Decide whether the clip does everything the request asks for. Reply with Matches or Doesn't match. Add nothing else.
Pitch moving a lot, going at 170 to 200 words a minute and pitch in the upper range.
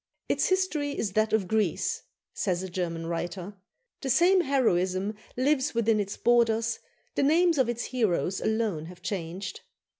Doesn't match